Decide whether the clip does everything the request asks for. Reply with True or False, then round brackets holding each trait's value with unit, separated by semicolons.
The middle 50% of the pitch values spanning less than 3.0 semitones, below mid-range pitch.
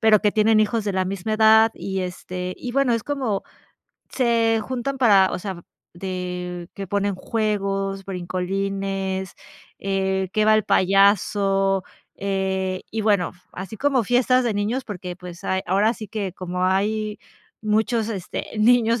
False (2.6 semitones; 200 Hz)